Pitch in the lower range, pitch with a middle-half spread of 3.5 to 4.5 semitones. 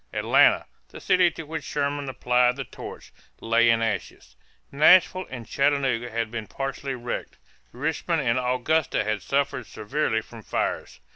Yes: low, 130 Hz; average, 3.9 semitones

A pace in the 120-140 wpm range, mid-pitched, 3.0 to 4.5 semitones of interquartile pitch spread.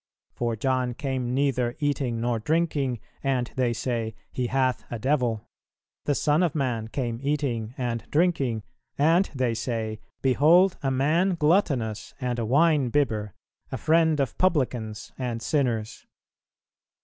No: slow, 135 wpm; low, 130 Hz; average, 3.9 semitones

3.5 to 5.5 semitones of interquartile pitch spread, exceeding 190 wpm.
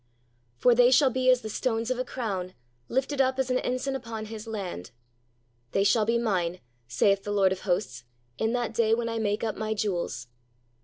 Yes: average, 3.8 semitones; average, 200 wpm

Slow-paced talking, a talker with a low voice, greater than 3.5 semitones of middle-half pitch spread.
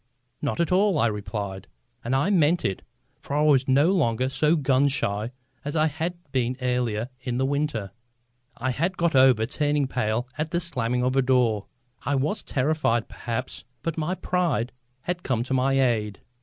No: average, 185 wpm; low, 130 Hz; average, 4.4 semitones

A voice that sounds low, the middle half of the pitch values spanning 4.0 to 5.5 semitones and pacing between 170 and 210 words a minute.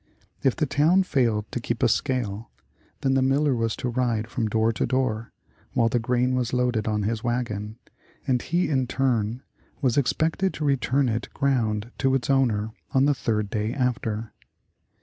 No: low, 125 Hz; average, 3.2 semitones; average, 175 wpm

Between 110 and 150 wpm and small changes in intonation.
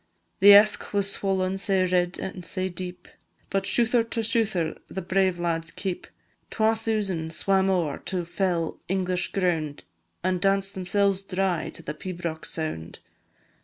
Yes: average, 145 wpm; narrow, 2.2 semitones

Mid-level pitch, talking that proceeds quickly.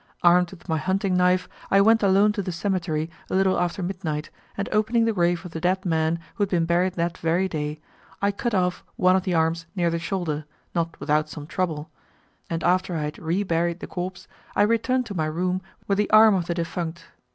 Yes: medium, 180 Hz; fast, 220 wpm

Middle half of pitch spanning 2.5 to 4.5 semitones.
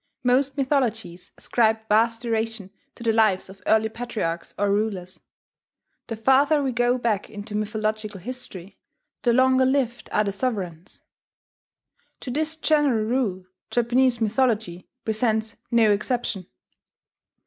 Yes: average, 3.2 semitones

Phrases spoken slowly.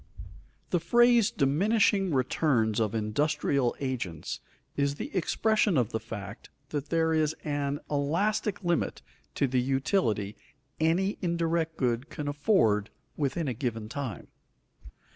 Yes: slow, 125 wpm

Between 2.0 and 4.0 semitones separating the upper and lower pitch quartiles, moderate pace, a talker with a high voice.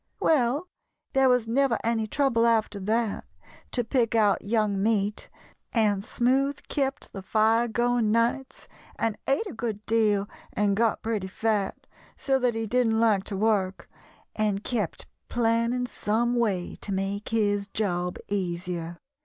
Yes: average, 2.8 semitones; average, 145 wpm; high, 225 Hz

